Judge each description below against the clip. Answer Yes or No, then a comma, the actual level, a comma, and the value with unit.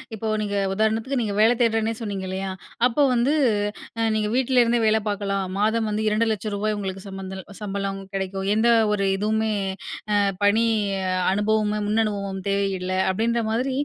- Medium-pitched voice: No, high, 210 Hz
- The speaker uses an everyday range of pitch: No, narrow, 2.2 semitones